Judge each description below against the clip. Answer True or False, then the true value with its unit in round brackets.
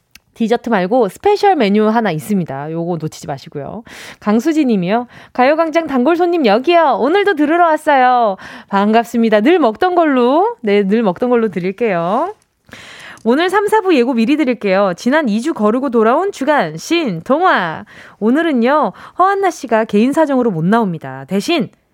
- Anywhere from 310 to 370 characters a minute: True (325 characters per minute)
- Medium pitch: False (240 Hz)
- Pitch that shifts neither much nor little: False (7.7 semitones)